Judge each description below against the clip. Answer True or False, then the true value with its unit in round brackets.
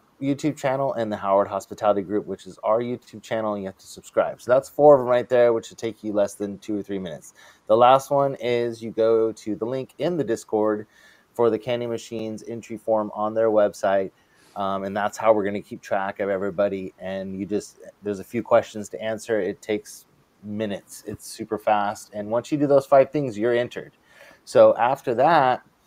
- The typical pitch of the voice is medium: False (110 Hz)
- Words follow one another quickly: True (215 wpm)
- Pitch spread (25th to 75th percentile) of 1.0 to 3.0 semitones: True (2.7 semitones)